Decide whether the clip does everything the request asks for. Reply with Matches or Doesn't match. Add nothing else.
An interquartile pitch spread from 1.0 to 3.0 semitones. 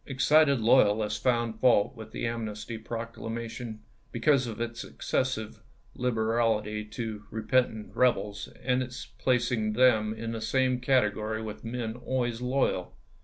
Matches